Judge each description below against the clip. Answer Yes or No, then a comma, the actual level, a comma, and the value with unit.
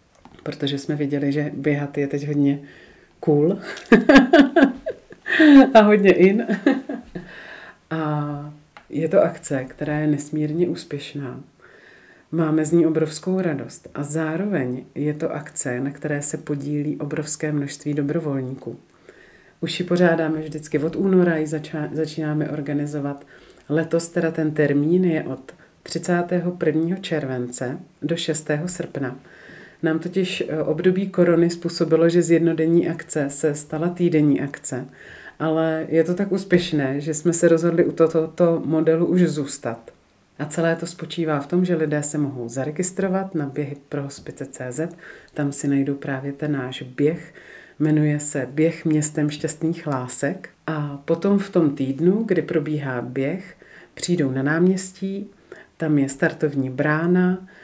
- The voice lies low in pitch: No, medium, 155 Hz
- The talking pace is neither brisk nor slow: Yes, average, 135 wpm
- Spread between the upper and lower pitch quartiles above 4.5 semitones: No, average, 2.7 semitones